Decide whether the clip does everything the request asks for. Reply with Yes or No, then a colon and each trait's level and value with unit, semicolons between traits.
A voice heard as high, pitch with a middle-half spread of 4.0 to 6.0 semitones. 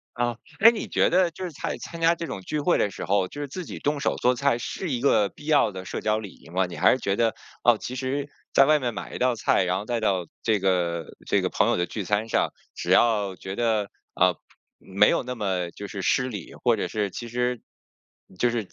No: low, 115 Hz; wide, 5.5 semitones